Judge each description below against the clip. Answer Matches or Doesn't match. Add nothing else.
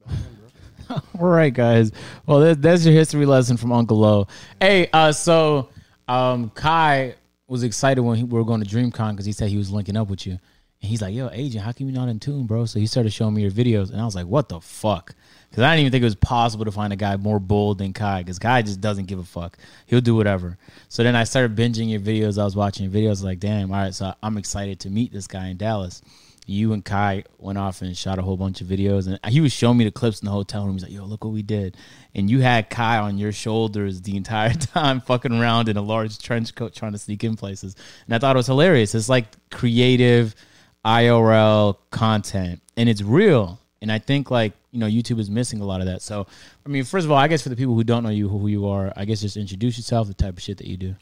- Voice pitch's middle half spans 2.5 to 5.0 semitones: Matches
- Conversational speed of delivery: Doesn't match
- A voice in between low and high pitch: Doesn't match